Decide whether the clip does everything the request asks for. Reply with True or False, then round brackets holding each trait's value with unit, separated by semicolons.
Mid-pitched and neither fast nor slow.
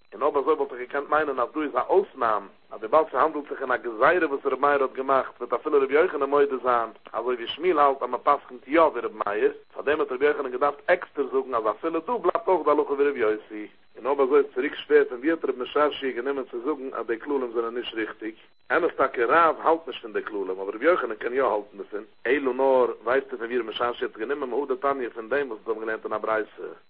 False (150 Hz; 240 wpm)